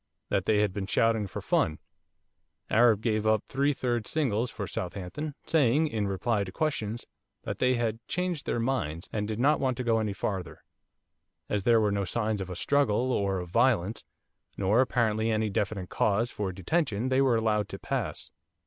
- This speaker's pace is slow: No, average, 185 wpm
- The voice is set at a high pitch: No, low, 110 Hz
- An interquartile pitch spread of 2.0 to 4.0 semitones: Yes, average, 3.7 semitones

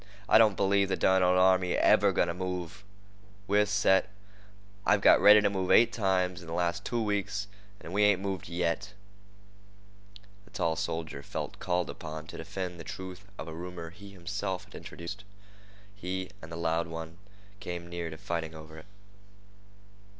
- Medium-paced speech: Yes, average, 170 wpm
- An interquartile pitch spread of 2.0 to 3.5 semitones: Yes, average, 2.8 semitones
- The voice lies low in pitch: Yes, very low, 90 Hz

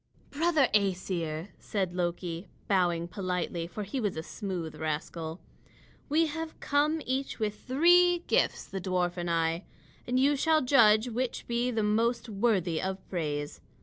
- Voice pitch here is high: Yes, high, 200 Hz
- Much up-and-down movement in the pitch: Yes, wide, 6.7 semitones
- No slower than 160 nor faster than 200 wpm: No, average, 150 wpm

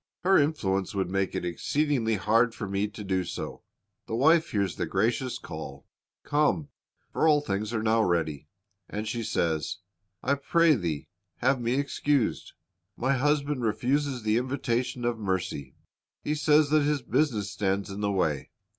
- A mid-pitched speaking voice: No, low, 115 Hz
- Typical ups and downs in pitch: No, wide, 6.5 semitones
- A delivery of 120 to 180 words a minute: Yes, average, 160 wpm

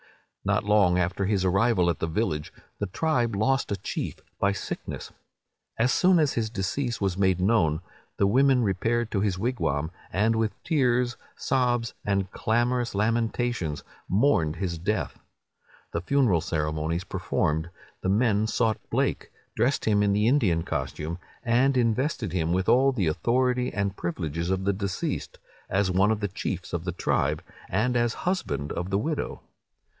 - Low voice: Yes, low, 105 Hz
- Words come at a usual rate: Yes, average, 160 wpm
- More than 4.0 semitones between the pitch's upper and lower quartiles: Yes, average, 4.9 semitones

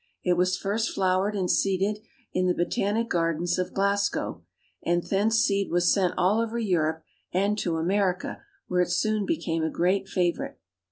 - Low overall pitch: No, medium, 185 Hz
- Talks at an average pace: Yes, average, 165 wpm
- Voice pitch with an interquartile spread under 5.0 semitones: Yes, narrow, 2.5 semitones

